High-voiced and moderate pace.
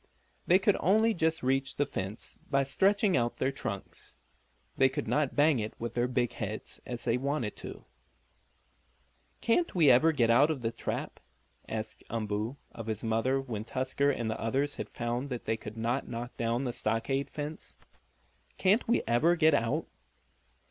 No: low, 130 Hz; average, 170 wpm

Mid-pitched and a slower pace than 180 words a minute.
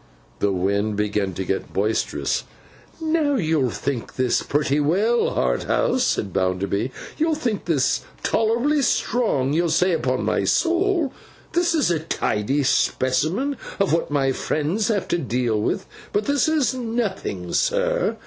Yes: medium, 165 Hz; average, 145 wpm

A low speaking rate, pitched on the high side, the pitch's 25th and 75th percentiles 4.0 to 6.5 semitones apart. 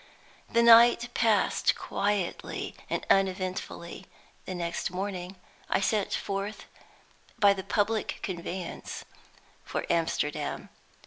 No: slow, 100 wpm; high, 195 Hz; narrow, 2.6 semitones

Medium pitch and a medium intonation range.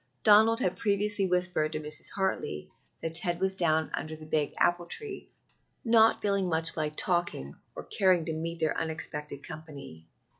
Yes: medium, 165 Hz; average, 3.6 semitones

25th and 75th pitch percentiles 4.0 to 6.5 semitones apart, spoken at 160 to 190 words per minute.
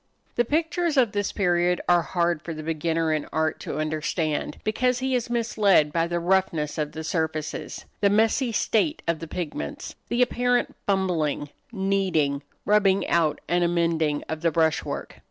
Yes: average, 4.8 semitones; average, 165 wpm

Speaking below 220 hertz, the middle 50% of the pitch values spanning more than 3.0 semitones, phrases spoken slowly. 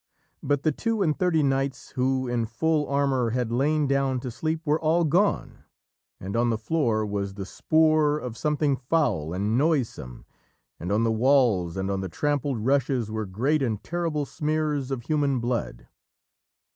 No: low, 135 Hz; average, 5.0 semitones; average, 170 wpm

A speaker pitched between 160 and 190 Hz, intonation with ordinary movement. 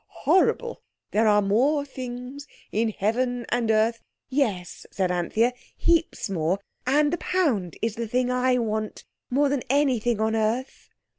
No: high, 240 Hz; average, 3.9 semitones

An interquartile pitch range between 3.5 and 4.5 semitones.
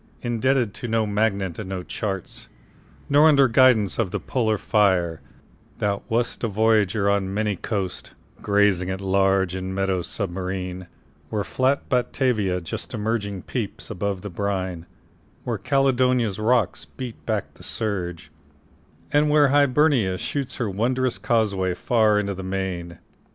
Yes: average, 4.1 semitones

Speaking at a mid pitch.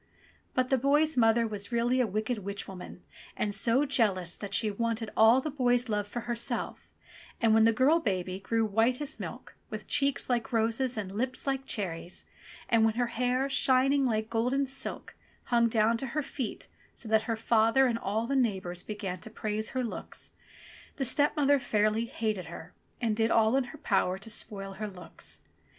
No: high, 230 Hz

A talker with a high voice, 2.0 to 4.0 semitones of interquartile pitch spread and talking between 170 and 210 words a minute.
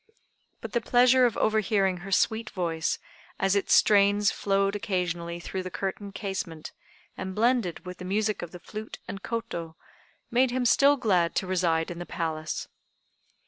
No: high, 195 Hz; average, 3.7 semitones; average, 160 wpm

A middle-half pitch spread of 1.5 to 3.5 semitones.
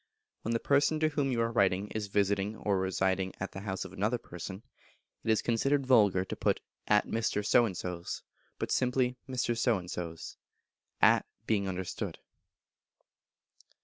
No: average, 4.0 semitones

